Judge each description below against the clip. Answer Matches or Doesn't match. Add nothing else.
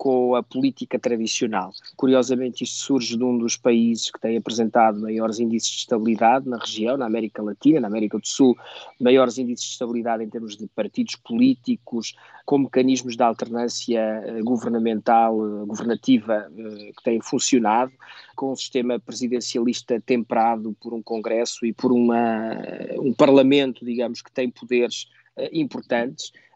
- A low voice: Matches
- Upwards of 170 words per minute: Doesn't match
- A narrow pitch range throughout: Matches